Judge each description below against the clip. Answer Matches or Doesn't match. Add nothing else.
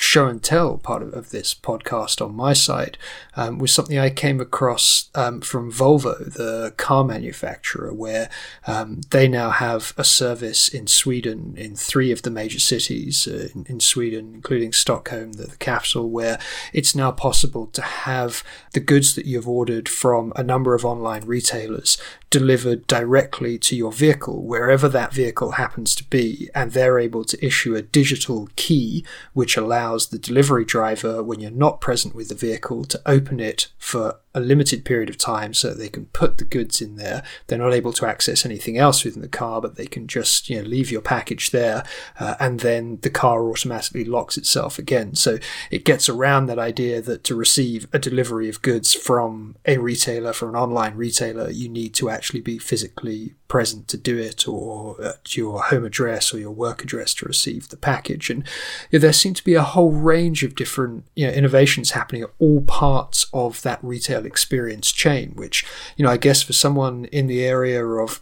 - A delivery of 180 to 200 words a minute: Matches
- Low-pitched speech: Matches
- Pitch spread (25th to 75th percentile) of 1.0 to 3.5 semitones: Matches